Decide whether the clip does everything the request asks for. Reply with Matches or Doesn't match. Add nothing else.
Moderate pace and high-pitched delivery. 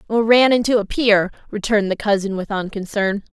Matches